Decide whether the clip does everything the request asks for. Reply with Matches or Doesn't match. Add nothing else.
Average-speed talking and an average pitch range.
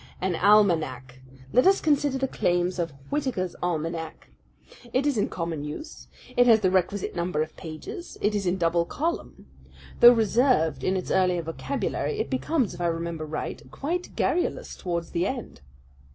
Doesn't match